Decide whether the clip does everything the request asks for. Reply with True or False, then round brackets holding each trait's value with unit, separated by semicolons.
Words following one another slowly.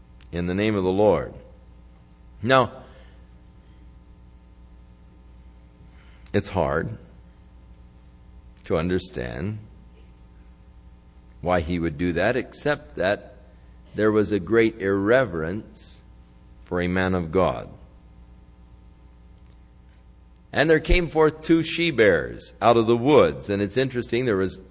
True (105 wpm)